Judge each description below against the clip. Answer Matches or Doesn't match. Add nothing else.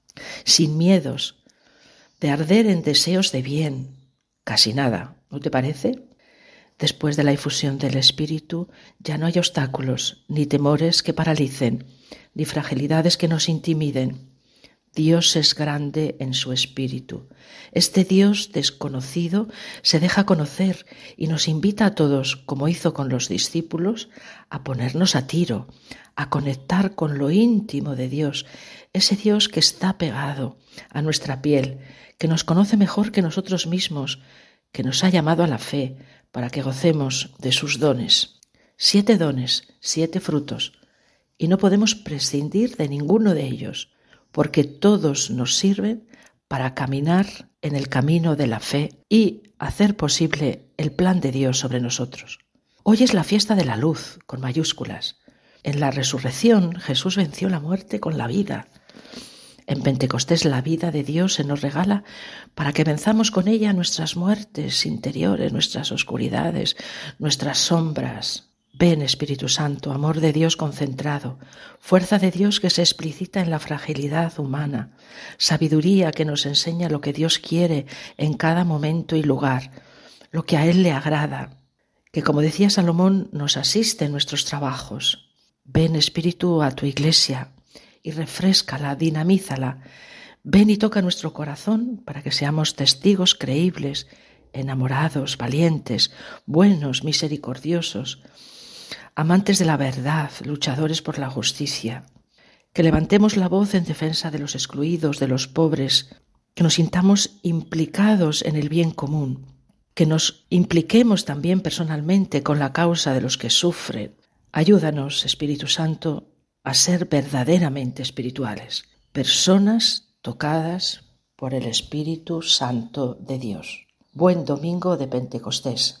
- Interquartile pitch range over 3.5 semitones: Matches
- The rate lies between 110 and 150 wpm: Matches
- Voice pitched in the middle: Matches